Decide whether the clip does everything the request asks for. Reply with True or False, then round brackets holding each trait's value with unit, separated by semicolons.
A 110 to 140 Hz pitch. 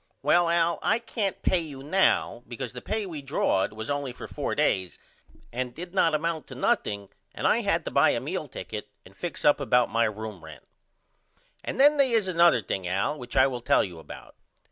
True (135 Hz)